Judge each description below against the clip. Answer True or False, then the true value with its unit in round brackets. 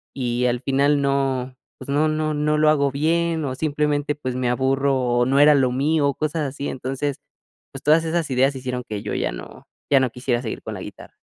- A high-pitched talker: False (140 Hz)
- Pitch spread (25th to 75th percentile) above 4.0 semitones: False (2.7 semitones)